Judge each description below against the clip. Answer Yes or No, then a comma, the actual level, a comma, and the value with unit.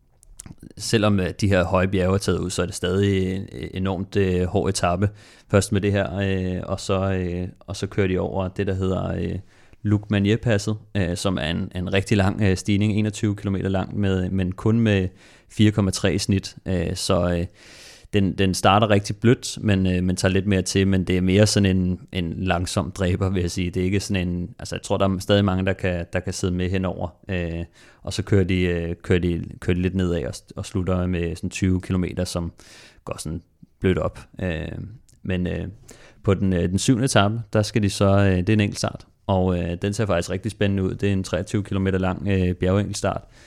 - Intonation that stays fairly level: Yes, narrow, 1.9 semitones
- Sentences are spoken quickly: No, average, 215 wpm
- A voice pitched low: Yes, very low, 95 Hz